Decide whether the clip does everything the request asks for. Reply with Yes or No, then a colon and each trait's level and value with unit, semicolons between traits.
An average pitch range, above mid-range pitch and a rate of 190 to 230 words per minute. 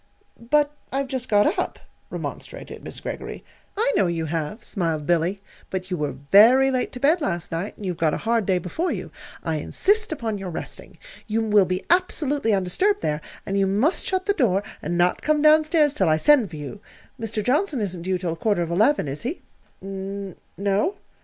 No: wide, 8.4 semitones; high, 205 Hz; average, 200 wpm